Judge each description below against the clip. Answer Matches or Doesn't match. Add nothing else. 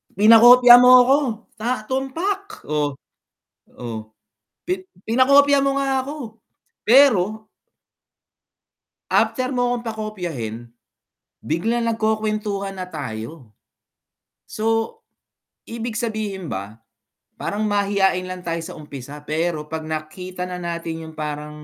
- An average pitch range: Doesn't match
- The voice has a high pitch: Matches